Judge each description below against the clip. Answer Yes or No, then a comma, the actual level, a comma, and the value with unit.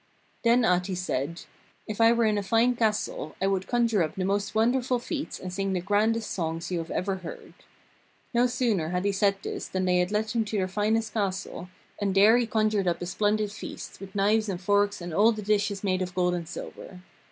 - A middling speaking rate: No, fast, 215 wpm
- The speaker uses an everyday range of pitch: Yes, average, 3.1 semitones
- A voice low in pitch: No, high, 200 Hz